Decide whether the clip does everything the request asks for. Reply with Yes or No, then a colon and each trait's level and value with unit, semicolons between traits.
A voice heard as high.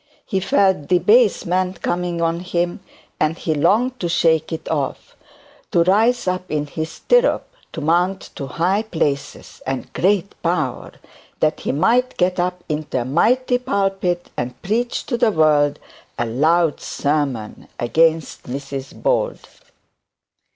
No: medium, 170 Hz